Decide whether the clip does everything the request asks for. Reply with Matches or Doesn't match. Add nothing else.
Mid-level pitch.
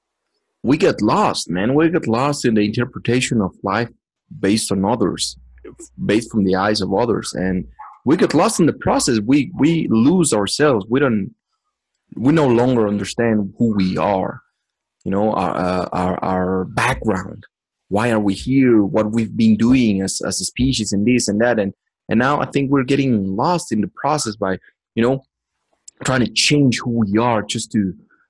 Doesn't match